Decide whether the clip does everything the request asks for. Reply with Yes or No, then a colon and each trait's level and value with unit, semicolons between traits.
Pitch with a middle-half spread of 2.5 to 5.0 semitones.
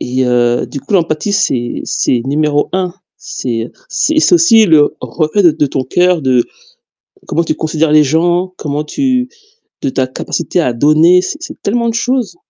No: wide, 5.5 semitones